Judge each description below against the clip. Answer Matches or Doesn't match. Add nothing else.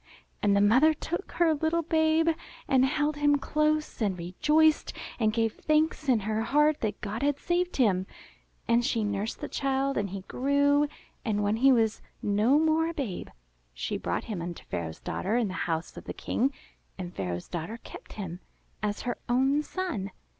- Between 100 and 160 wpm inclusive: Doesn't match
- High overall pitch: Matches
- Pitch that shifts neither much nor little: Doesn't match